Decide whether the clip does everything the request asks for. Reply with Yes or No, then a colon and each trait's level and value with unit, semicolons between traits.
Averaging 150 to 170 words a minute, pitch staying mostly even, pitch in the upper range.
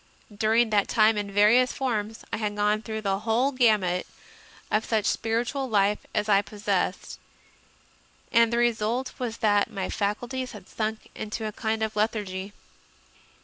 Yes: average, 155 wpm; narrow, 1.9 semitones; high, 215 Hz